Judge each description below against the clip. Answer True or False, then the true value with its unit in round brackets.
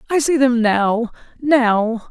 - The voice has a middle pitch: False (245 Hz)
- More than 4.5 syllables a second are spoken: False (3.3 syllables/s)